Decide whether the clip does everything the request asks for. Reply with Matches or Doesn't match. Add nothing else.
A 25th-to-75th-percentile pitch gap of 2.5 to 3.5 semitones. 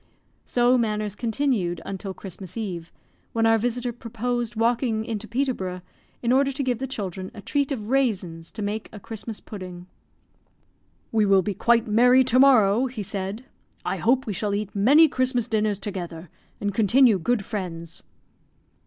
Doesn't match